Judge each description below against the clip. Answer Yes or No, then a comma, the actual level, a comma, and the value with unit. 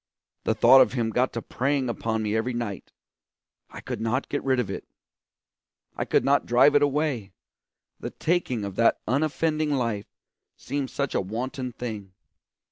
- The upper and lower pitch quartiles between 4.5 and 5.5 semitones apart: No, average, 3.9 semitones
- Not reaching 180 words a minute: Yes, average, 165 wpm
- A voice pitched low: Yes, low, 125 Hz